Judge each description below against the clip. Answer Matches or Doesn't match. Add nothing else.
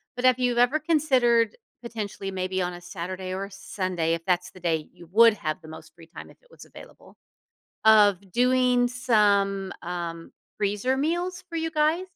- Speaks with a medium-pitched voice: Doesn't match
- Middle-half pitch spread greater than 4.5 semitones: Matches